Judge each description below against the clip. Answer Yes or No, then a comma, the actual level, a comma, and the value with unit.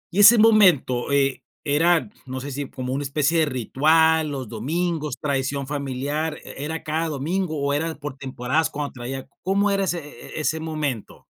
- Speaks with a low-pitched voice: No, medium, 150 Hz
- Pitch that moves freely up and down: No, average, 3.2 semitones